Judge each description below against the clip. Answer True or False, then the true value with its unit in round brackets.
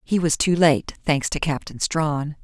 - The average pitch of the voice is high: False (155 Hz)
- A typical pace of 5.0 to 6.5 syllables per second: False (4.2 syllables/s)